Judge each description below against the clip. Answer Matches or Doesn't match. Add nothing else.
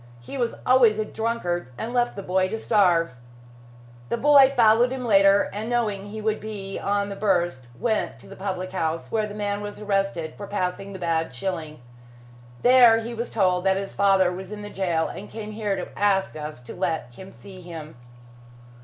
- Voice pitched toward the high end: Matches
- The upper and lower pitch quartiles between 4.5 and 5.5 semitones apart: Doesn't match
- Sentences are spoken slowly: Doesn't match